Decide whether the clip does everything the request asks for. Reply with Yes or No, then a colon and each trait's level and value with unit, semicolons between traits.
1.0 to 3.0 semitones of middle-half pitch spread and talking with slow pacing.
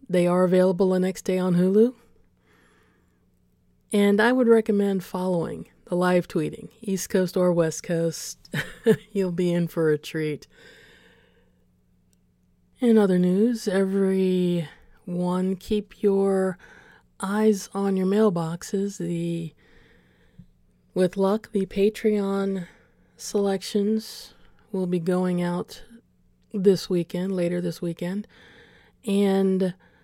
Yes: narrow, 2.5 semitones; slow, 105 wpm